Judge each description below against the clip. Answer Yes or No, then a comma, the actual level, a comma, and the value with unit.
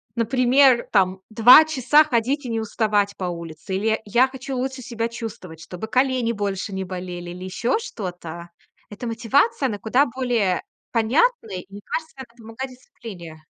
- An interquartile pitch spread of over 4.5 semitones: Yes, average, 5.2 semitones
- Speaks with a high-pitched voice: Yes, high, 225 Hz